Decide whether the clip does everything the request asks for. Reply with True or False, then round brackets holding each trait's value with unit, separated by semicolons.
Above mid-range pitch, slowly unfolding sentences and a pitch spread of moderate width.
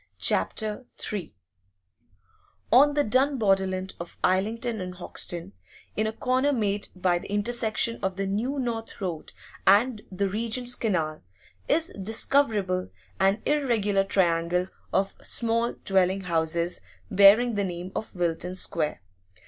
True (200 Hz; 125 wpm; 4.1 semitones)